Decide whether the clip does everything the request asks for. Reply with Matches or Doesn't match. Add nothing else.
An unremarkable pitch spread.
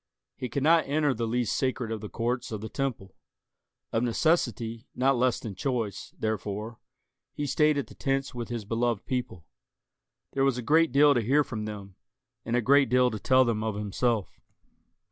Matches